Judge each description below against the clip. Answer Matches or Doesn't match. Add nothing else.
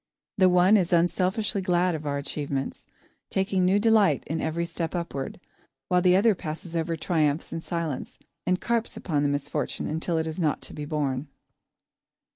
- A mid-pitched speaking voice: Matches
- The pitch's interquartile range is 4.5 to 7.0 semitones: Doesn't match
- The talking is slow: Doesn't match